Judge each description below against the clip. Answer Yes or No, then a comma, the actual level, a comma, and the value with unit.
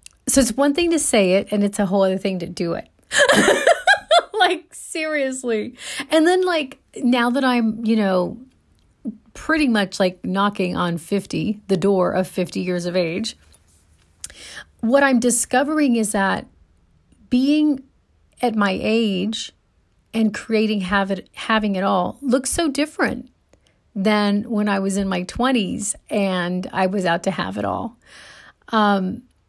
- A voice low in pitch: No, high, 215 Hz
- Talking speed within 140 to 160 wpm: Yes, average, 150 wpm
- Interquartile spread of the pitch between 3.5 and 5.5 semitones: Yes, average, 5.2 semitones